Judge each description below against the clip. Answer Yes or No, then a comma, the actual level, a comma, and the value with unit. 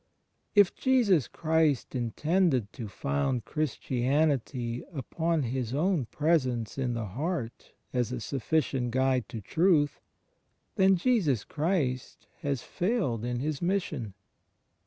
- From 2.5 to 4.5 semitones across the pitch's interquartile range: No, average, 5.3 semitones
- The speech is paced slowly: Yes, slow, 120 wpm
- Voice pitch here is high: No, low, 135 Hz